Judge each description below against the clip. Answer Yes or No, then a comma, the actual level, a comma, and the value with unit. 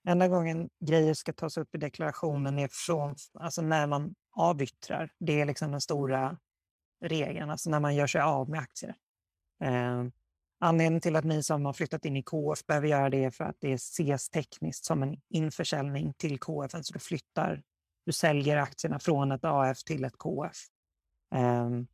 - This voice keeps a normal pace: Yes, average, 185 wpm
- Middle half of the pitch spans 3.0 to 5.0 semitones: Yes, average, 3.3 semitones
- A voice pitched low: No, medium, 150 Hz